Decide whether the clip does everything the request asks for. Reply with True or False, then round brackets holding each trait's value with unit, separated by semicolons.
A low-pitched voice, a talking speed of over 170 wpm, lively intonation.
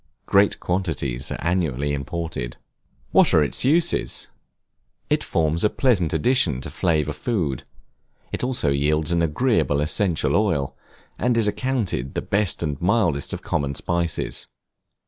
False (85 Hz; 135 wpm; 6.2 semitones)